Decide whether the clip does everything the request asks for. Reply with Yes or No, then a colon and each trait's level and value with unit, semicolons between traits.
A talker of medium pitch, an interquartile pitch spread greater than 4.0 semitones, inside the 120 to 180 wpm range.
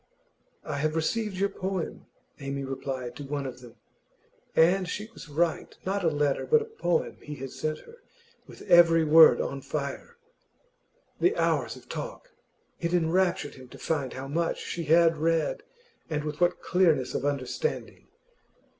Yes: medium, 160 Hz; average, 4.6 semitones; average, 160 wpm